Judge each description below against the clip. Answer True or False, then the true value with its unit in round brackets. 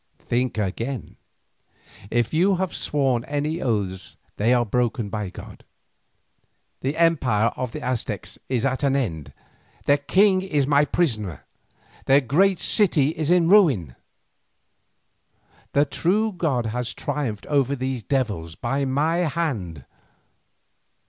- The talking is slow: True (125 wpm)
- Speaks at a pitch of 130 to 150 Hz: True (135 Hz)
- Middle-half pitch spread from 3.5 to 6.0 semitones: True (5.4 semitones)